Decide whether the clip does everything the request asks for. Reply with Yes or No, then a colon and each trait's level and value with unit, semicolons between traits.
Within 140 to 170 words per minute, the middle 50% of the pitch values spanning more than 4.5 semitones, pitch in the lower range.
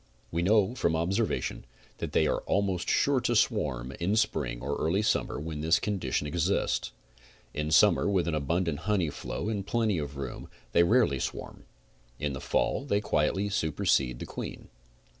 Yes: average, 165 wpm; wide, 5.6 semitones; very low, 85 Hz